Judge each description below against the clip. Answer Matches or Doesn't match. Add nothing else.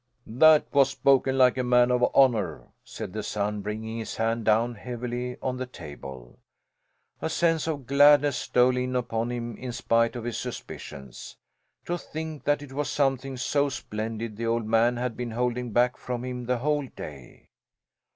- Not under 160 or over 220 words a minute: Matches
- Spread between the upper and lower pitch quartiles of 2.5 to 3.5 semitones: Matches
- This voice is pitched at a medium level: Doesn't match